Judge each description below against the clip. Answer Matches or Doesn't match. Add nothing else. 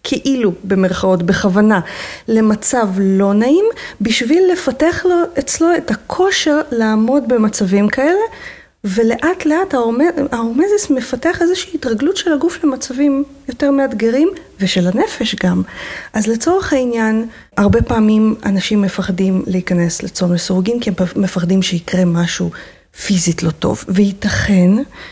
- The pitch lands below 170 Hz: Doesn't match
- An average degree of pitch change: Doesn't match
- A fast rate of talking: Doesn't match